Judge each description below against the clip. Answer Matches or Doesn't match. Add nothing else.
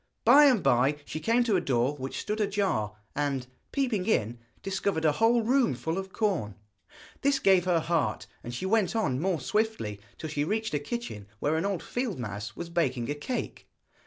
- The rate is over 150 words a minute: Matches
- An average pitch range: Doesn't match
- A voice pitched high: Doesn't match